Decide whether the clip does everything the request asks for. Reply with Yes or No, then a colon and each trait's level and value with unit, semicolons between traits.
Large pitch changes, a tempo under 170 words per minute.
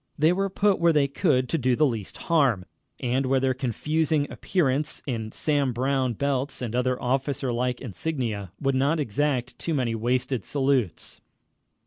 No: average, 3.0 semitones; average, 155 wpm